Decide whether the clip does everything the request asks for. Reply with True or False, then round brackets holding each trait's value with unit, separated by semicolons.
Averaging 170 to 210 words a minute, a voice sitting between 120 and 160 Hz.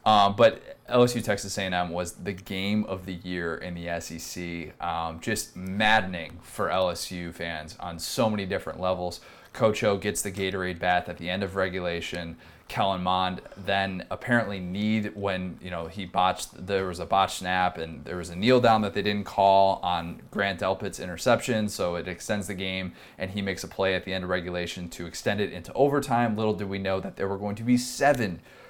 False (200 wpm; 95 Hz)